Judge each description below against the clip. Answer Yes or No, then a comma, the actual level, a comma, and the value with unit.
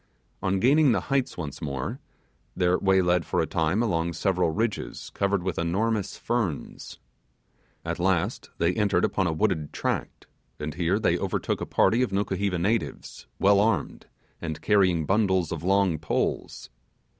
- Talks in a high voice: No, very low, 95 Hz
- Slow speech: No, average, 155 wpm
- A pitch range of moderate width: Yes, average, 3.5 semitones